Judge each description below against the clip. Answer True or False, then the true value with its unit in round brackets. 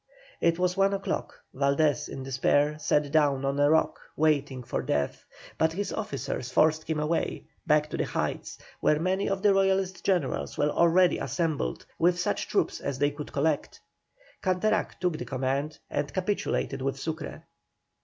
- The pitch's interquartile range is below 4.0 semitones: False (4.4 semitones)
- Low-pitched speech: False (155 Hz)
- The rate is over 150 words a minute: True (165 wpm)